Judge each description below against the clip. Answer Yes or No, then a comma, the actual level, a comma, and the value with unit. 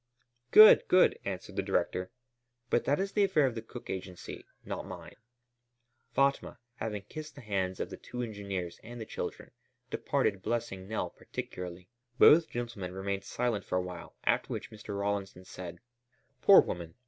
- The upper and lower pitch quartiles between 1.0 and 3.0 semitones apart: No, average, 4.8 semitones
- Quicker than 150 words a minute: Yes, average, 160 wpm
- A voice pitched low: Yes, low, 100 Hz